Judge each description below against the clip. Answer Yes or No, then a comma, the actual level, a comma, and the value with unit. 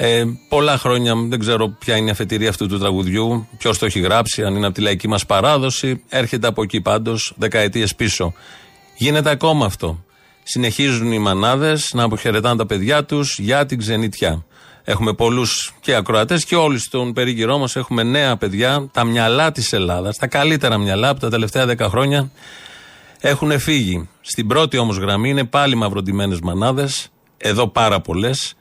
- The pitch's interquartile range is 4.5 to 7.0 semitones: No, average, 4.0 semitones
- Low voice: Yes, low, 115 Hz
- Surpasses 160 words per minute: Yes, fast, 170 wpm